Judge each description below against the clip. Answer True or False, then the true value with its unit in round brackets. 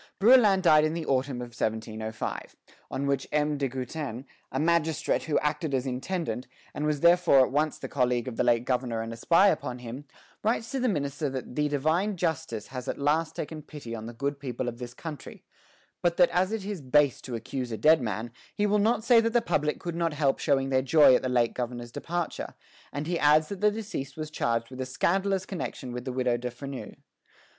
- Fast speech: True (220 wpm)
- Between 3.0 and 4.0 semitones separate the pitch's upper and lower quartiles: False (5.1 semitones)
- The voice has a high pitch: False (140 Hz)